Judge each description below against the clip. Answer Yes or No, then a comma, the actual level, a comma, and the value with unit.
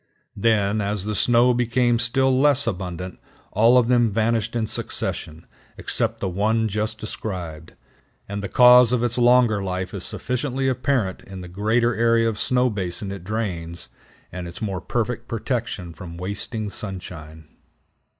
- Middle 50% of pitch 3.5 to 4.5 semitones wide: Yes, average, 4.2 semitones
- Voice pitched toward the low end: Yes, low, 110 Hz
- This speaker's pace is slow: No, average, 150 wpm